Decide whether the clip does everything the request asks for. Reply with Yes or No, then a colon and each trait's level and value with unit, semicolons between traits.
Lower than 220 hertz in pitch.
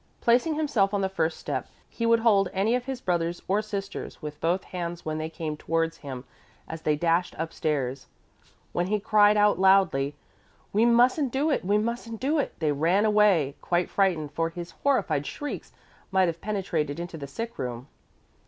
Yes: medium, 185 Hz